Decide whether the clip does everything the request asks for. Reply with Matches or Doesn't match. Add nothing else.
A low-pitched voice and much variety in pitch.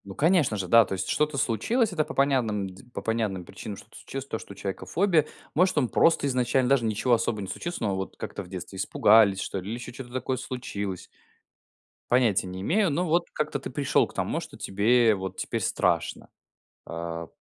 Matches